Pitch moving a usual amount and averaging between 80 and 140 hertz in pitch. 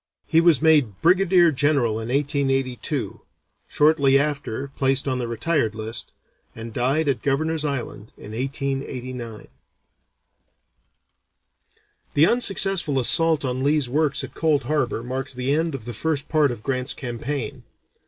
Yes: average, 3.8 semitones; low, 135 Hz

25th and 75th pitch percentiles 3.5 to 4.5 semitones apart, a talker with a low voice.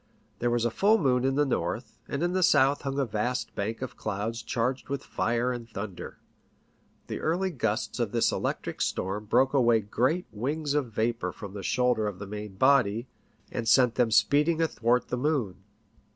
Yes: average, 4.2 semitones; low, 120 Hz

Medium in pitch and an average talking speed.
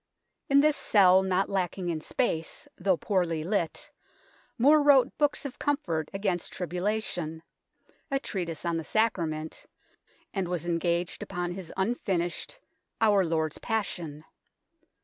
No: medium, 180 Hz; slow, 130 wpm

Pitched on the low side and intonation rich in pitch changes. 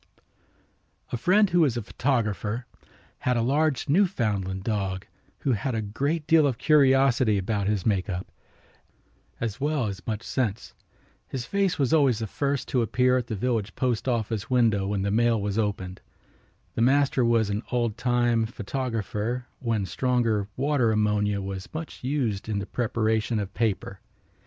No: low, 115 Hz; average, 4.0 semitones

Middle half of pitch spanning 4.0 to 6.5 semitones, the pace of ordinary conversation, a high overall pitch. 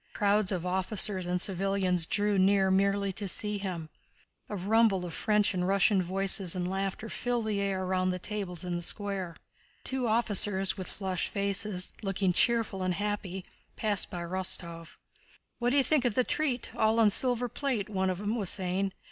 No: narrow, 2.4 semitones; average, 175 wpm; high, 195 Hz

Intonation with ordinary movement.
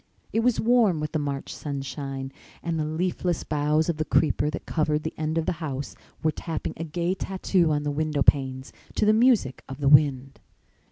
Yes: average, 3.1 semitones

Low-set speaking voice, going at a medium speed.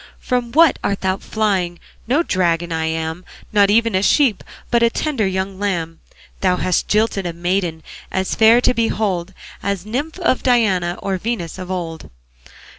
No: high, 195 Hz; average, 165 wpm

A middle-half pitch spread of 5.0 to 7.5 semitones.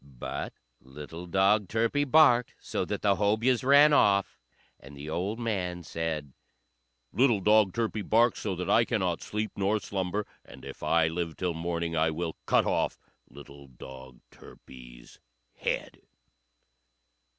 Yes: average, 5.3 semitones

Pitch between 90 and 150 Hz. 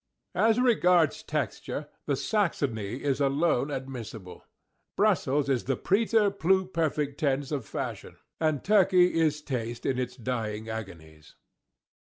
Yes: medium, 140 Hz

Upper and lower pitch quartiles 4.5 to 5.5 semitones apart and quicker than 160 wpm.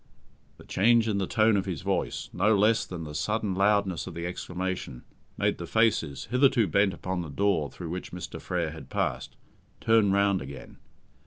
No: average, 3.8 semitones; average, 180 wpm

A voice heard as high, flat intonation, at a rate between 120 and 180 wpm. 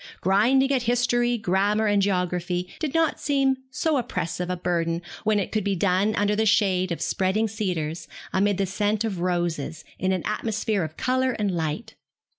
No: high, 200 Hz; average, 3.8 semitones; average, 175 wpm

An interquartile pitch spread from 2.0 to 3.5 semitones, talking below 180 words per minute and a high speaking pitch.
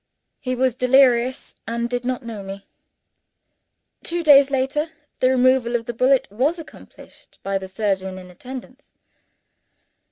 Yes: average, 2.9 semitones; slow, 135 wpm; very high, 250 Hz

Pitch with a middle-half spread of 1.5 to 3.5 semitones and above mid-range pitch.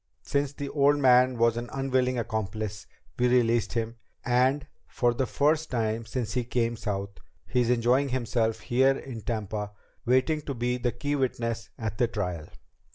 No: narrow, 2.6 semitones; low, 120 Hz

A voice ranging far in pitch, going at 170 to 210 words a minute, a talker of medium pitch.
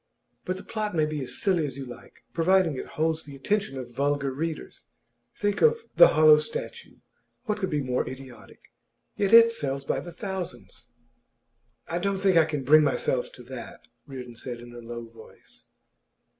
Yes: wide, 6.5 semitones; average, 175 wpm; medium, 150 Hz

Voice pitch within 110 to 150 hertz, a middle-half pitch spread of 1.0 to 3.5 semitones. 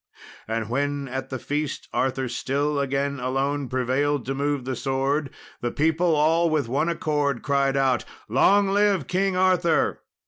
Yes: medium, 140 Hz; average, 2.8 semitones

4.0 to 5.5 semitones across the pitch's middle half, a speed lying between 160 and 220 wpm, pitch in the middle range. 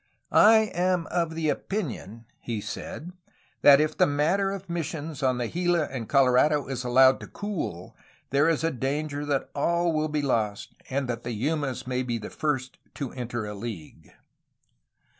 Yes: average, 4.7 semitones; average, 165 wpm; medium, 145 Hz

